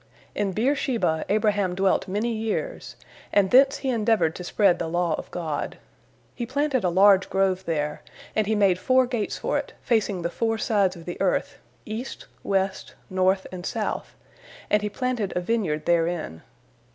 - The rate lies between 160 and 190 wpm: Yes, average, 170 wpm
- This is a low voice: No, high, 195 Hz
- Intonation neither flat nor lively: Yes, average, 4.0 semitones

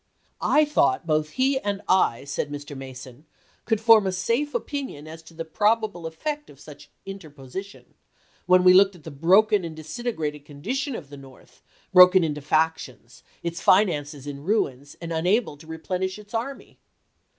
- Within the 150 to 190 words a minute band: Yes, average, 175 wpm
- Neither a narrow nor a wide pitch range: No, wide, 6.2 semitones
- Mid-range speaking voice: Yes, medium, 170 Hz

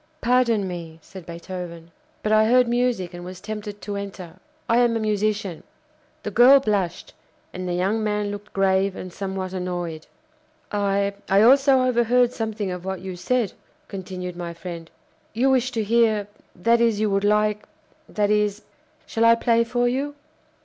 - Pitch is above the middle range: Yes, high, 205 Hz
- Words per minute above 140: Yes, average, 165 wpm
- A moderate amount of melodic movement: Yes, average, 3.8 semitones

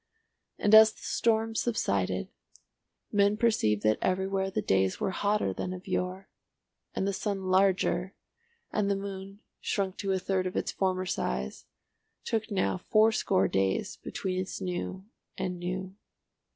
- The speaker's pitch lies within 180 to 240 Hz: Yes, high, 190 Hz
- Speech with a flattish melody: Yes, narrow, 1.7 semitones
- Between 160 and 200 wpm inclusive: No, average, 145 wpm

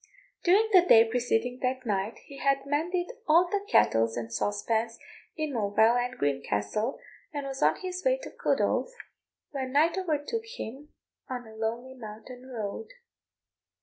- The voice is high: Yes, very high, 255 Hz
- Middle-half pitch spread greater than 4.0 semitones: Yes, wide, 5.6 semitones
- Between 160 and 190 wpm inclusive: No, average, 150 wpm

